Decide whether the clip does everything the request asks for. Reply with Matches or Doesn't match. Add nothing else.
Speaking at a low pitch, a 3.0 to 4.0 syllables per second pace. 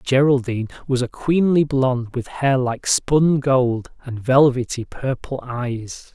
Matches